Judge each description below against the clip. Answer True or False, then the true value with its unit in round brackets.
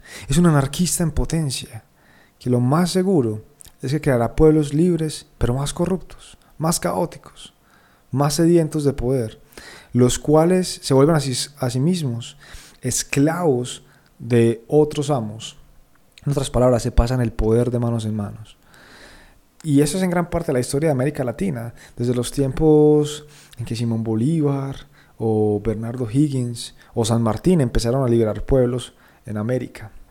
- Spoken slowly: False (155 wpm)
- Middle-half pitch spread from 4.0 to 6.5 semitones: True (4.4 semitones)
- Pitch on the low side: True (130 Hz)